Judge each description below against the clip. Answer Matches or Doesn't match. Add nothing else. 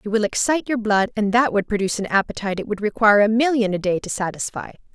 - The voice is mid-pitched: Doesn't match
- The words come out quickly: Matches